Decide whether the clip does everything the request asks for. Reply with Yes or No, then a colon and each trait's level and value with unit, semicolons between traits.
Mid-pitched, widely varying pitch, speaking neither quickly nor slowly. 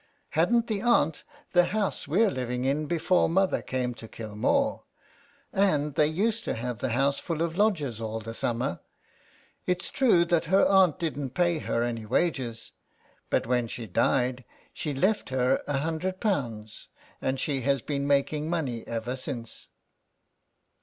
Yes: medium, 145 Hz; wide, 6.3 semitones; average, 160 wpm